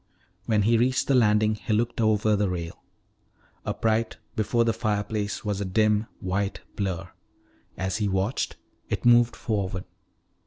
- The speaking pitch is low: Yes, low, 105 Hz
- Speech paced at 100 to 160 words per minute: Yes, average, 145 wpm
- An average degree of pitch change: No, narrow, 2.3 semitones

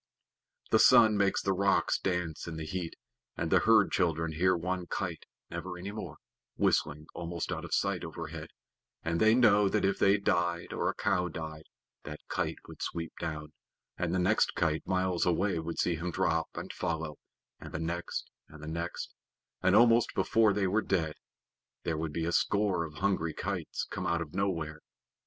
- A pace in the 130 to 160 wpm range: No, average, 185 wpm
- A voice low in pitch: Yes, very low, 85 Hz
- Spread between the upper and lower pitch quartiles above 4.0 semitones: No, average, 3.2 semitones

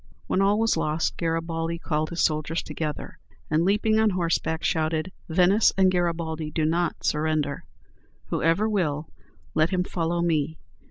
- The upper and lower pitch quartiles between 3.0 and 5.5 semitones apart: No, narrow, 2.5 semitones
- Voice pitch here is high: No, medium, 165 Hz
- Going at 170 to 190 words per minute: No, average, 145 wpm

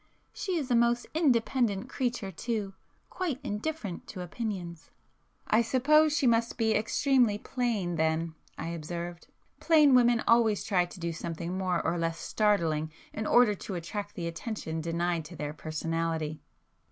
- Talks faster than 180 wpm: No, average, 145 wpm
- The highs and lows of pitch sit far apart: Yes, wide, 6.2 semitones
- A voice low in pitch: No, high, 205 Hz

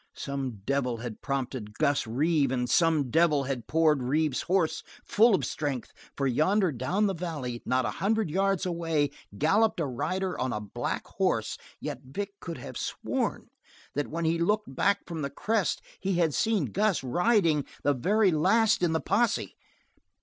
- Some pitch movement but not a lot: No, wide, 6.0 semitones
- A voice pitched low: No, medium, 160 Hz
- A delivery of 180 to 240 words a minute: No, average, 170 wpm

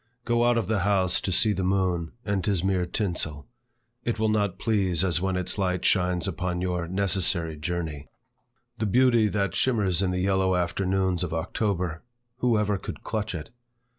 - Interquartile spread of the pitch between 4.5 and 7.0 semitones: No, average, 2.7 semitones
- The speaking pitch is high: No, very low, 95 Hz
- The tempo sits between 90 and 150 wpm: No, average, 180 wpm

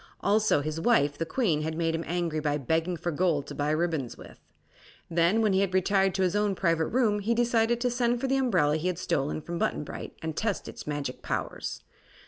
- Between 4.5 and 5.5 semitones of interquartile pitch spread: Yes, average, 5.2 semitones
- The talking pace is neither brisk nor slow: No, fast, 220 wpm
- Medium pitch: Yes, medium, 175 Hz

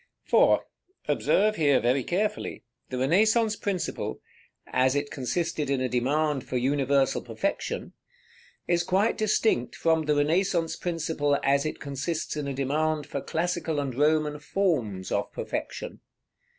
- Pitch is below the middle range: No, medium, 150 Hz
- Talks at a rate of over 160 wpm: No, average, 140 wpm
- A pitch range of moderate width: Yes, average, 4.0 semitones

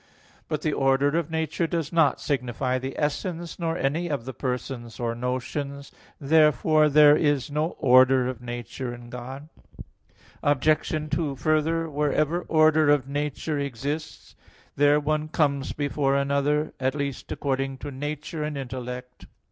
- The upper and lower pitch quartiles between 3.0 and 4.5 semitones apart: No, narrow, 2.6 semitones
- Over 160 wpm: No, average, 140 wpm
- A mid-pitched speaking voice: Yes, medium, 145 Hz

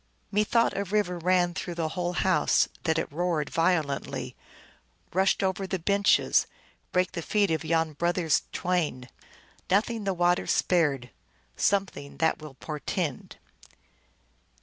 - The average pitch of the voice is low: No, medium, 175 Hz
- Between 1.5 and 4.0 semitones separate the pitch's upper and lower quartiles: Yes, average, 2.9 semitones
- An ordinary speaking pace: No, slow, 130 wpm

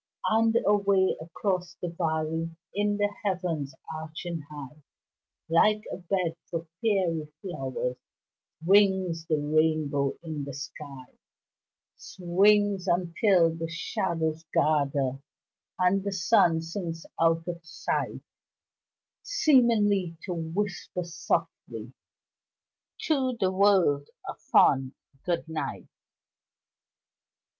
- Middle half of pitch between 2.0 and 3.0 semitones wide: No, average, 3.8 semitones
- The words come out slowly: Yes, slow, 100 wpm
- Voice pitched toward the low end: No, medium, 170 Hz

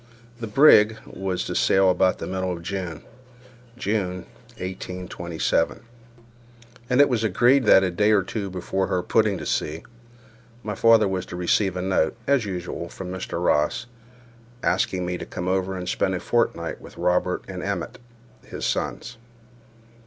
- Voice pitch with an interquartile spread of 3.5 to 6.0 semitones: No, average, 2.7 semitones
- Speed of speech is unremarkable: Yes, average, 160 wpm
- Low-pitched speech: Yes, very low, 95 Hz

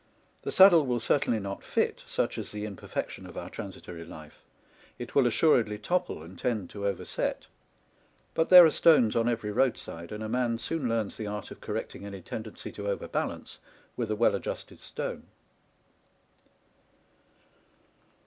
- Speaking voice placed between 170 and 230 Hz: No, low, 110 Hz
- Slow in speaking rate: No, average, 160 wpm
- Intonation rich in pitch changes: No, average, 3.6 semitones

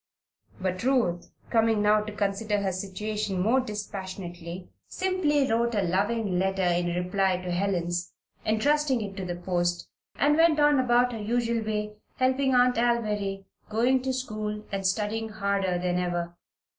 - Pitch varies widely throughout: No, average, 4.2 semitones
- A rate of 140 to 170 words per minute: Yes, average, 150 wpm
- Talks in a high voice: Yes, high, 210 Hz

